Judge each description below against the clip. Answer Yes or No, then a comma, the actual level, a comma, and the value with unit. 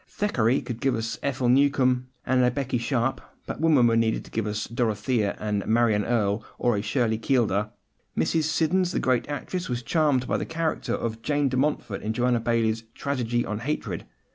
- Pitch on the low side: Yes, low, 120 Hz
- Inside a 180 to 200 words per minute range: Yes, average, 195 wpm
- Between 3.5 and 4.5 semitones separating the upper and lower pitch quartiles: Yes, average, 3.8 semitones